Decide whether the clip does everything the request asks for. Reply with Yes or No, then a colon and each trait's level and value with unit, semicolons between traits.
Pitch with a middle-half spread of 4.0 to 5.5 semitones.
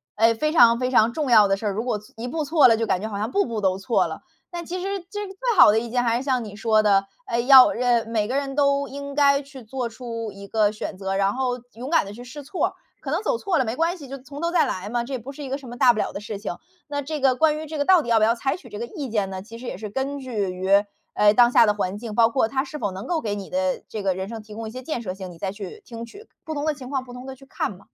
Yes: average, 4.8 semitones